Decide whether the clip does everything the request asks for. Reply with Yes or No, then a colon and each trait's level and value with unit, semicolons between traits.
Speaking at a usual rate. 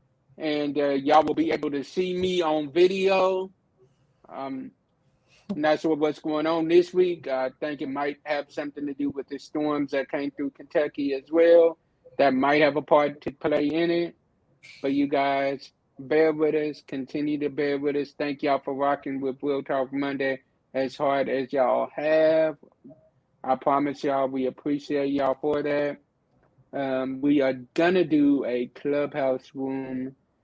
Yes: average, 170 wpm